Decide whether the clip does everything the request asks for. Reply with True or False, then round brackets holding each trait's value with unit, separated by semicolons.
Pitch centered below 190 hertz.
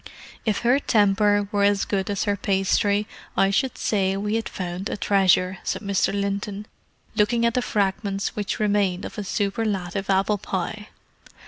False (200 Hz)